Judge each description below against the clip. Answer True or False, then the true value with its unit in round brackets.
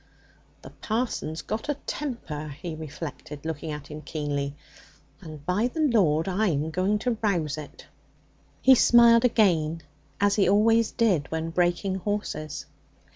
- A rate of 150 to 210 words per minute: False (135 wpm)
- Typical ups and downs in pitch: False (6.0 semitones)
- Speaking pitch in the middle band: True (175 Hz)